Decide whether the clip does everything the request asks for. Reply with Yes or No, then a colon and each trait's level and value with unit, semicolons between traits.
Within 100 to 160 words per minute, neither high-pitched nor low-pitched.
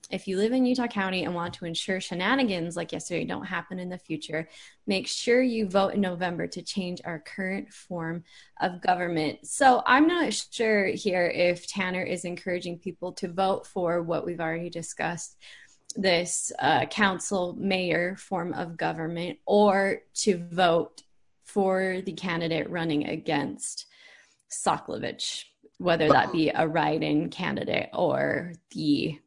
Yes: average, 150 wpm; medium, 180 Hz